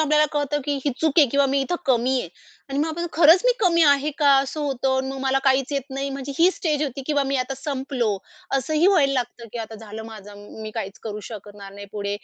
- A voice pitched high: Yes, very high, 270 Hz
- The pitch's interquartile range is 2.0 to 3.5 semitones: No, average, 4.1 semitones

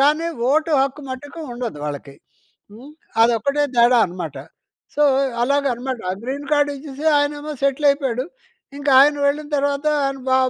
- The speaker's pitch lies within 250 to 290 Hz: Yes, very high, 275 Hz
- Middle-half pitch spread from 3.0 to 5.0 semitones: No, narrow, 2.6 semitones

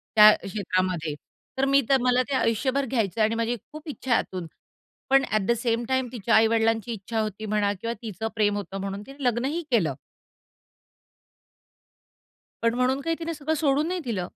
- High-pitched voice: Yes, high, 230 Hz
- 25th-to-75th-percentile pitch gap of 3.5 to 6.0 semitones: Yes, average, 4.0 semitones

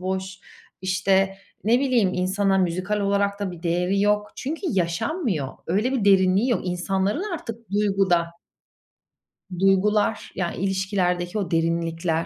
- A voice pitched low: No, high, 195 Hz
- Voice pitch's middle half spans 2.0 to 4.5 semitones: Yes, narrow, 2.5 semitones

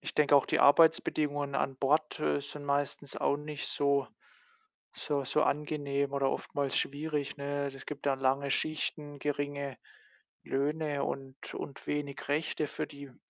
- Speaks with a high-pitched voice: No, medium, 140 Hz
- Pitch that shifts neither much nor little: No, narrow, 1.1 semitones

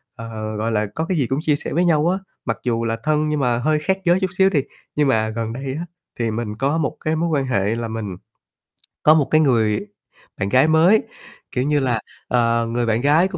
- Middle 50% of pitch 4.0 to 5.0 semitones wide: No, wide, 5.4 semitones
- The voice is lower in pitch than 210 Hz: Yes, low, 135 Hz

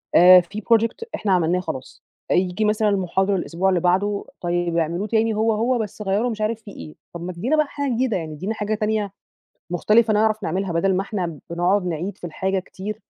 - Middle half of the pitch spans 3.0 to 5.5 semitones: Yes, average, 3.5 semitones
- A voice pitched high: Yes, high, 195 Hz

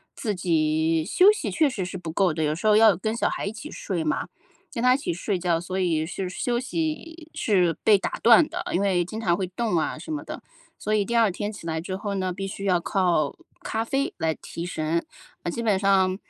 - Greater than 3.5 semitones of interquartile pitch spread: Yes, average, 4.6 semitones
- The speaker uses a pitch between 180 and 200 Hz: Yes, high, 190 Hz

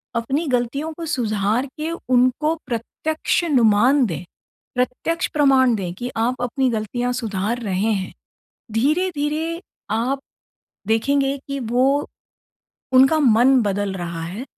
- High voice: Yes, very high, 250 Hz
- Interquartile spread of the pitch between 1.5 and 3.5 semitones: No, average, 4.2 semitones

